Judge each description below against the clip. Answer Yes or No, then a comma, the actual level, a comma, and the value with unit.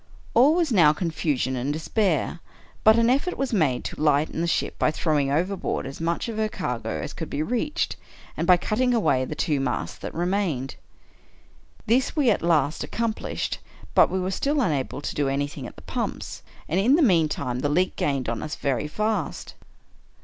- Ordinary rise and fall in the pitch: No, wide, 7.3 semitones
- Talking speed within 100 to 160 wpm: No, average, 195 wpm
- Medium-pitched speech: Yes, medium, 165 Hz